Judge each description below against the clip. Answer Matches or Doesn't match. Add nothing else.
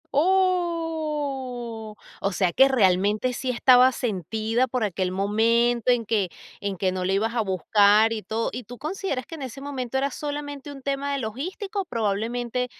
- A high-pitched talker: Matches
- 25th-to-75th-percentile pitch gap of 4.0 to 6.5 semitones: Matches